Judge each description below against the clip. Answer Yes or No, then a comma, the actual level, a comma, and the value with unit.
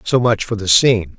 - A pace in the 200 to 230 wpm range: No, fast, 255 wpm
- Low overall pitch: Yes, low, 105 Hz